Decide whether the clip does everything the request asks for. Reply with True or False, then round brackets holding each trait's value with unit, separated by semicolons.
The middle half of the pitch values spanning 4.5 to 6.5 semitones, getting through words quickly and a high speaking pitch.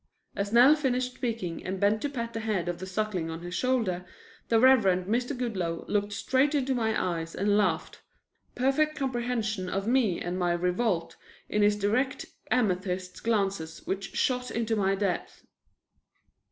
False (5.1 semitones; 160 wpm; 210 Hz)